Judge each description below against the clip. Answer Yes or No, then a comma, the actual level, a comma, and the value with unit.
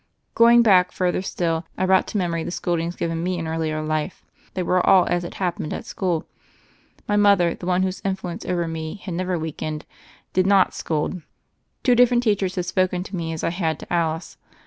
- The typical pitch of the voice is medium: Yes, medium, 180 Hz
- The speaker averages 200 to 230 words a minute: Yes, fast, 205 wpm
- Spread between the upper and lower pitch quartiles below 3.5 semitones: Yes, narrow, 2.5 semitones